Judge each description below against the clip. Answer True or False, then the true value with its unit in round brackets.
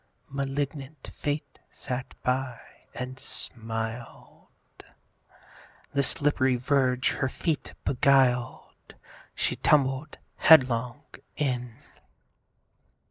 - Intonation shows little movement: True (2.3 semitones)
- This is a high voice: False (130 Hz)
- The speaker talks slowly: True (75 wpm)